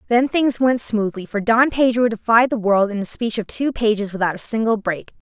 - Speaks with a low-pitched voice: No, high, 225 Hz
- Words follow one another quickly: Yes, fast, 225 wpm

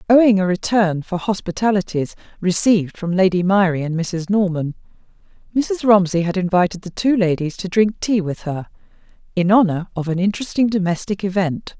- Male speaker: No, female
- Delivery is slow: No, average, 160 wpm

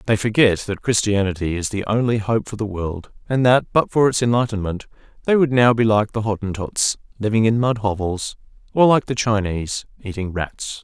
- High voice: No, low, 110 Hz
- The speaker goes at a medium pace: Yes, average, 190 wpm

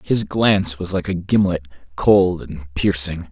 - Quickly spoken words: No, average, 165 wpm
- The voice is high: No, very low, 90 Hz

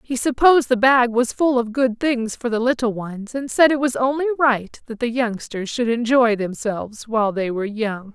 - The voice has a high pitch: Yes, high, 240 Hz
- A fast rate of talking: Yes, fast, 215 wpm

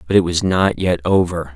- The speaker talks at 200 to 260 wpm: Yes, fast, 230 wpm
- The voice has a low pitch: Yes, very low, 90 Hz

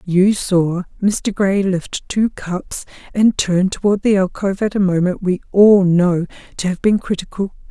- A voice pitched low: No, high, 190 Hz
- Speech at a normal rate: Yes, average, 170 wpm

